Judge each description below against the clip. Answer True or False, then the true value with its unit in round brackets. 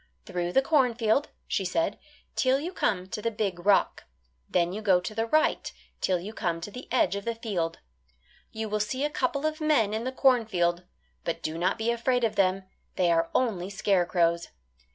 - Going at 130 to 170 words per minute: False (195 wpm)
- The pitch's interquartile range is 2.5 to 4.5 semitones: False (5.4 semitones)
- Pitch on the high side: True (210 Hz)